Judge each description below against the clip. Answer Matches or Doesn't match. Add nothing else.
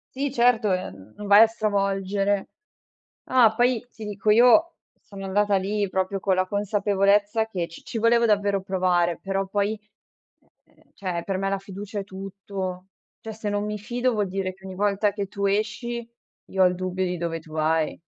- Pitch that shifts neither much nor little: Doesn't match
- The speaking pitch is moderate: Doesn't match